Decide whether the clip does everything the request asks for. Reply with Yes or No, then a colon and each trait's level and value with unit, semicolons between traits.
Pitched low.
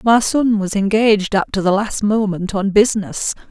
No: high, 205 Hz